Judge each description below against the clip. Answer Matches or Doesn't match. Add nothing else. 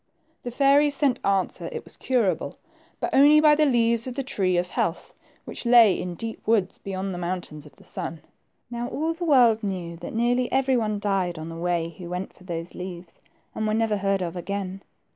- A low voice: Doesn't match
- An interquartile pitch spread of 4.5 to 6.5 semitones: Matches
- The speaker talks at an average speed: Doesn't match